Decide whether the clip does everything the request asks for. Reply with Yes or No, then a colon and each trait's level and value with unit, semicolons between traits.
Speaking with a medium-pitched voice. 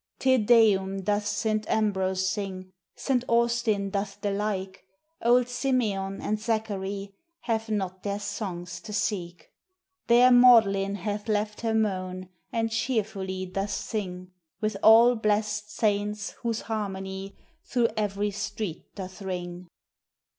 No: high, 205 Hz